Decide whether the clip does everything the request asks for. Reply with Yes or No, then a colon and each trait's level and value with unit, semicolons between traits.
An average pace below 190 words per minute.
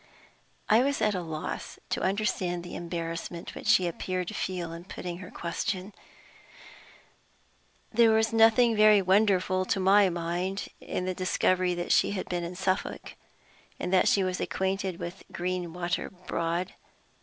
Yes: average, 150 wpm